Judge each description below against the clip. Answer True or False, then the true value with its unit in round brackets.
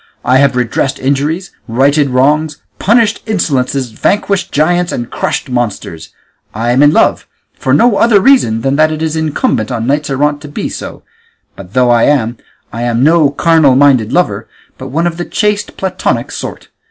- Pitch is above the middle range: False (140 Hz)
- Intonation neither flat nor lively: True (4.6 semitones)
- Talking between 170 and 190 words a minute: True (175 wpm)